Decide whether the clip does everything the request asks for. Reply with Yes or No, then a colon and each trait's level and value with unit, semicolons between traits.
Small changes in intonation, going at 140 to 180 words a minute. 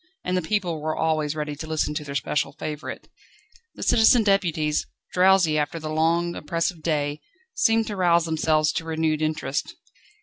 Yes: narrow, 2.2 semitones; average, 165 wpm